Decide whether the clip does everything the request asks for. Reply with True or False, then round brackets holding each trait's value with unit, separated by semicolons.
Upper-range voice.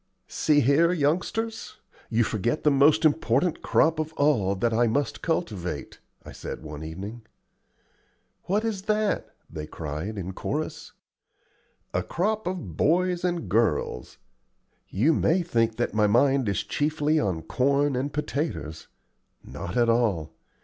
False (135 Hz)